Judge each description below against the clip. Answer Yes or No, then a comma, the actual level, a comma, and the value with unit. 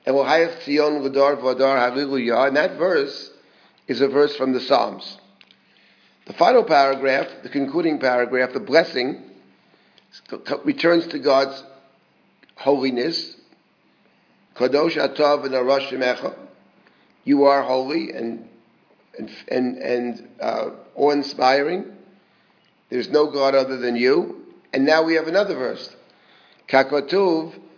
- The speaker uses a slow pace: Yes, slow, 90 wpm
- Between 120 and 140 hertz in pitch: Yes, low, 135 Hz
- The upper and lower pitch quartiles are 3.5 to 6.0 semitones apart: No, average, 2.7 semitones